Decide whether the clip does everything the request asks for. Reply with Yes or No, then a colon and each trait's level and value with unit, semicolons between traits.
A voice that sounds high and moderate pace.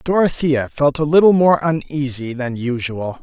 No: medium, 145 Hz; average, 150 wpm